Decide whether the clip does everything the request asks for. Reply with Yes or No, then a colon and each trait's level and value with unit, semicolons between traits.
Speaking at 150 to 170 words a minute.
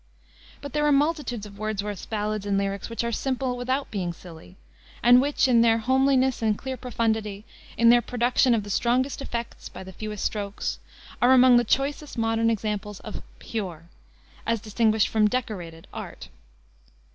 Yes: average, 165 wpm